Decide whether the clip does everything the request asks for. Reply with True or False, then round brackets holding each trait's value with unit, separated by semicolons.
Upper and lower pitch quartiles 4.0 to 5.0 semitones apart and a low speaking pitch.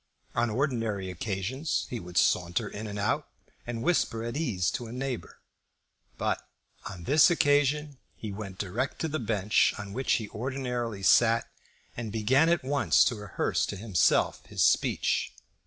True (4.7 semitones; 115 Hz)